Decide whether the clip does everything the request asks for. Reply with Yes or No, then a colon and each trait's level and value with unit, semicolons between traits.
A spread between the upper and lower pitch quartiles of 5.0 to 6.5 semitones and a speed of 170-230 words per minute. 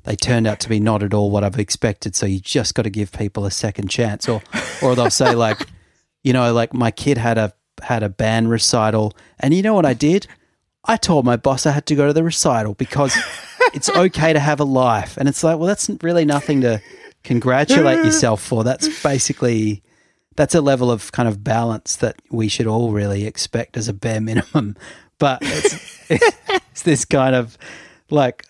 Yes: average, 5.3 semitones; fast, 205 wpm